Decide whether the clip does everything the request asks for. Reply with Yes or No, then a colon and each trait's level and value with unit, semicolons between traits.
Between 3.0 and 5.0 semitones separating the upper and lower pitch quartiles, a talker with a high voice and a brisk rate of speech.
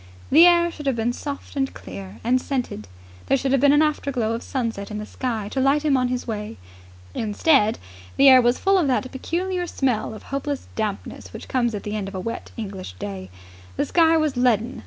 Yes: average, 4.7 semitones; very high, 255 Hz; fast, 215 wpm